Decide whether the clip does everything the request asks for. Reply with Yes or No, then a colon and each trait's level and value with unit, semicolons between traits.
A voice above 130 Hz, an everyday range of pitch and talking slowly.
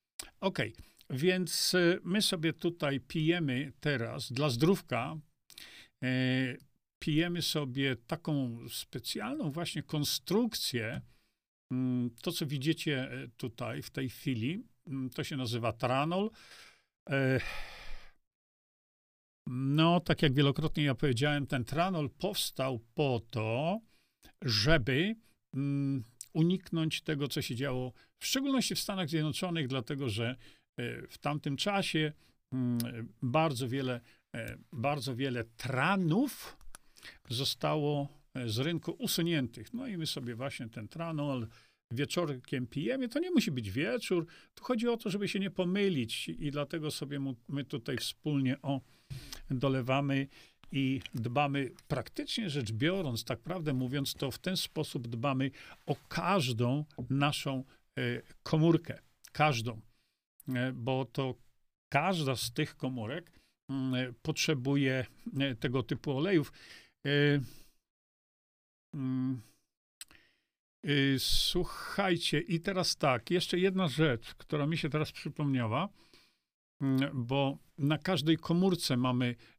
Yes: medium, 140 Hz; average, 4.2 semitones; slow, 105 wpm